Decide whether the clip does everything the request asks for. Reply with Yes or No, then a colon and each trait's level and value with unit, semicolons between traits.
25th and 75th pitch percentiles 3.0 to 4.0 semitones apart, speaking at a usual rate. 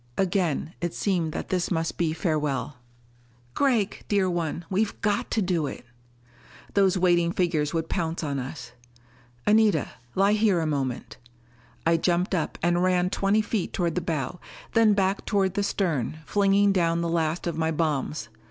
Yes: average, 3.5 semitones; average, 160 wpm